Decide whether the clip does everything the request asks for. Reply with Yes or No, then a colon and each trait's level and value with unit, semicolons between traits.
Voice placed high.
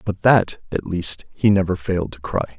No: very low, 95 Hz